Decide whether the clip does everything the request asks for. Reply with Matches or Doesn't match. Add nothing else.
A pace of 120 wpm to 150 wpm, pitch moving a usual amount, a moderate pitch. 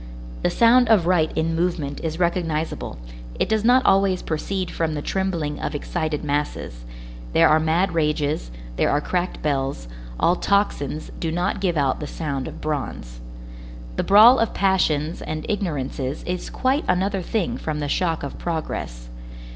Doesn't match